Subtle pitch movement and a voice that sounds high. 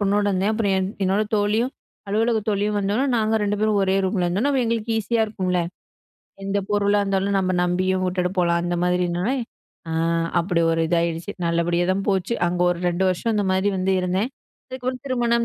No: average, 3.1 semitones; high, 195 Hz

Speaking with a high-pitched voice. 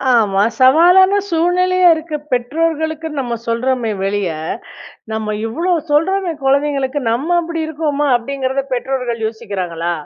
Yes: very high, 275 Hz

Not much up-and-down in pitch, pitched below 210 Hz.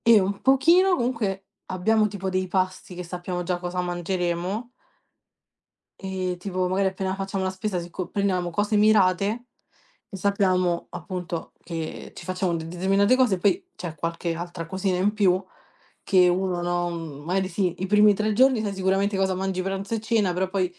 Yes: narrow, 2.2 semitones; high, 190 Hz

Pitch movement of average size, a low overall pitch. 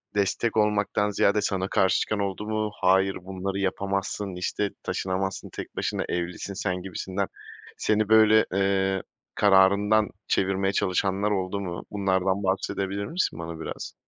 No: narrow, 1.6 semitones; very low, 95 Hz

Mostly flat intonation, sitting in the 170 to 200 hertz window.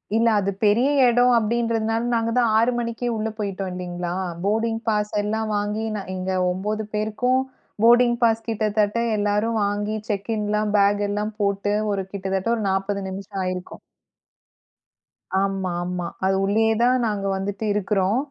No: narrow, 2.3 semitones; high, 210 Hz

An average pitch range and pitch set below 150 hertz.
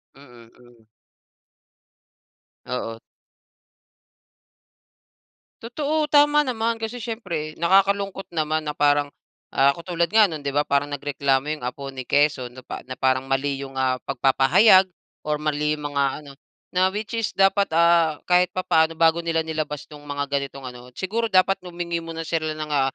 No: average, 5.0 semitones; medium, 155 Hz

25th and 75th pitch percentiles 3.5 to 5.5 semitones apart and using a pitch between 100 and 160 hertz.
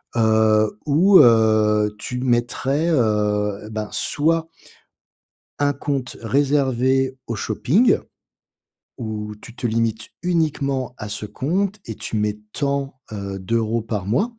Yes: average, 4.6 semitones; low, 120 Hz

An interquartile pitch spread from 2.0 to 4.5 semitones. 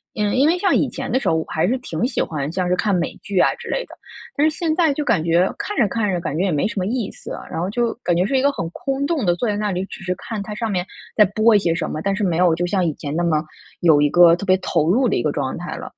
No: average, 5.3 semitones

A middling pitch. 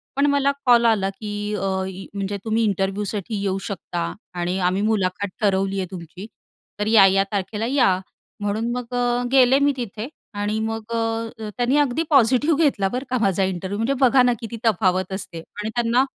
No: high, 210 Hz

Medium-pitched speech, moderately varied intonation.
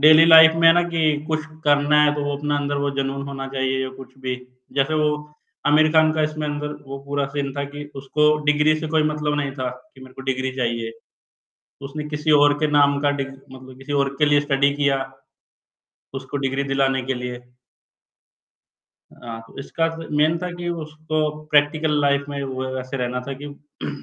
No: medium, 145 Hz; narrow, 2.0 semitones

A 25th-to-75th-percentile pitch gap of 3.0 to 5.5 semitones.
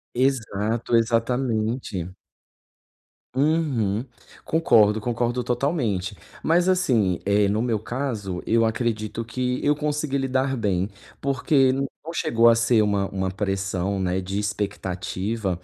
Yes: average, 4.6 semitones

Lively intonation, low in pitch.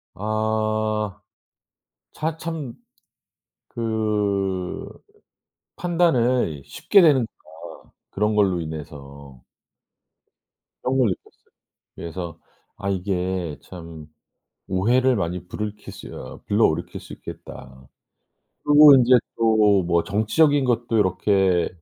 No: average, 5.0 semitones; low, 105 Hz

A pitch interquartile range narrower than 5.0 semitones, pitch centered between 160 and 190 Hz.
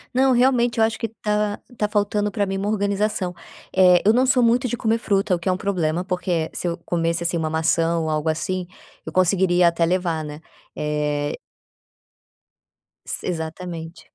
Yes: average, 4.0 semitones; medium, 185 Hz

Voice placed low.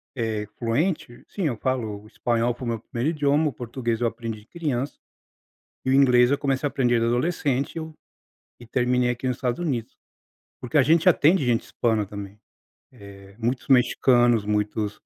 Yes: low, 125 Hz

